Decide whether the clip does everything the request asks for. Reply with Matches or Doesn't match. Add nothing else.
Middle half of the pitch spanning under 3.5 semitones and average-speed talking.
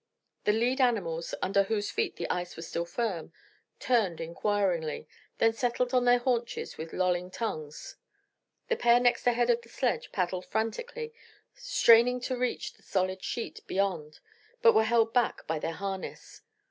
Doesn't match